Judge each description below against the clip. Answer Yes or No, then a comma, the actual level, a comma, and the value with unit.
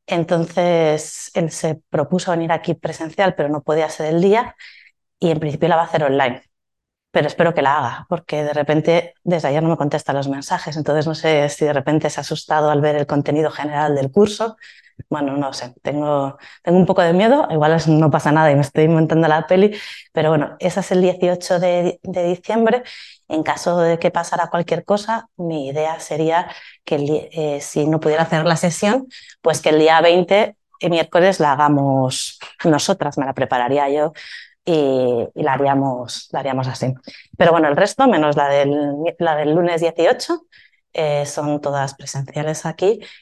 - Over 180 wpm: Yes, fast, 190 wpm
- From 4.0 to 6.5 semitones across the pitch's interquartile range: No, average, 3.0 semitones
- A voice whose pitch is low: No, medium, 160 Hz